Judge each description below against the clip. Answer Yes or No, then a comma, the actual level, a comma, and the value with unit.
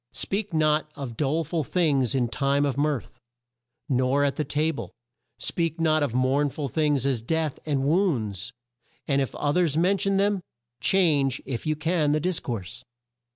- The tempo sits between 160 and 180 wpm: Yes, average, 175 wpm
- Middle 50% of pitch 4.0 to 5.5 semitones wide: No, average, 3.3 semitones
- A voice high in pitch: No, medium, 145 Hz